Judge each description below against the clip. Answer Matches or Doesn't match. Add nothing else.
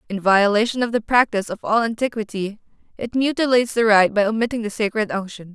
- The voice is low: Doesn't match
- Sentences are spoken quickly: Doesn't match